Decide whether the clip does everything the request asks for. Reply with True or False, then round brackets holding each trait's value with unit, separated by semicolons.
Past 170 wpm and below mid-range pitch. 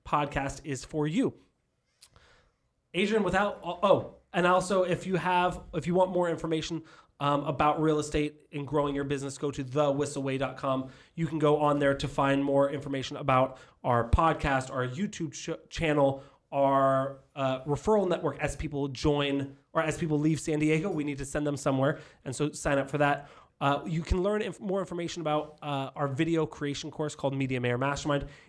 False (180 wpm; 145 Hz)